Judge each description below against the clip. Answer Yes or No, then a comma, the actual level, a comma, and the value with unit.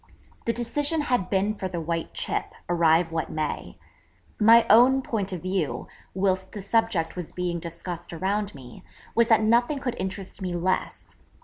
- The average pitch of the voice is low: No, high, 190 Hz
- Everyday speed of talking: Yes, average, 165 wpm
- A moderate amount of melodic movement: Yes, average, 4.7 semitones